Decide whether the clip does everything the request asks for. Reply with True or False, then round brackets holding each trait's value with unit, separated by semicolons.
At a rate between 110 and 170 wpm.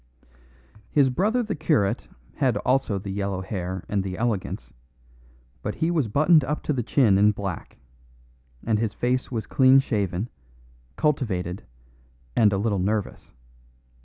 True (140 wpm)